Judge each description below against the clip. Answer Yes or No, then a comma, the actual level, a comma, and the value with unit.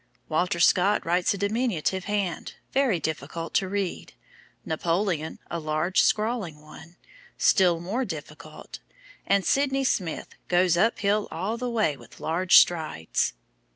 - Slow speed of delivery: Yes, slow, 130 wpm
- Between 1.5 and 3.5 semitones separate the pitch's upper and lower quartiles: No, average, 4.2 semitones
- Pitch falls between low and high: Yes, medium, 180 Hz